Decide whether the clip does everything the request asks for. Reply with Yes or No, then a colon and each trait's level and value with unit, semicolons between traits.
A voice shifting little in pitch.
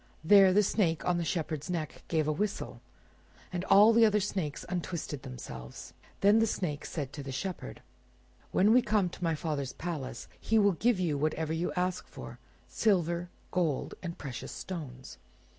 No: average, 4.4 semitones